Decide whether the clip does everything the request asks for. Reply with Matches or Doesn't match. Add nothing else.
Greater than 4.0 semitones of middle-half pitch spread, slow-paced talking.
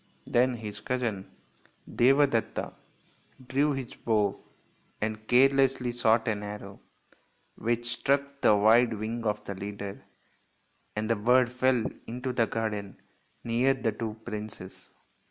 Doesn't match